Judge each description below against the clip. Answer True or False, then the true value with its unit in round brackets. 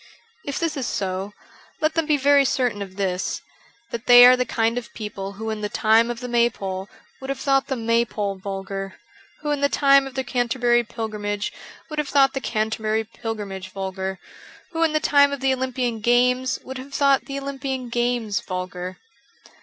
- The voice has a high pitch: True (240 Hz)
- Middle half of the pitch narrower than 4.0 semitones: False (4.6 semitones)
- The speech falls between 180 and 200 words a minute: True (190 wpm)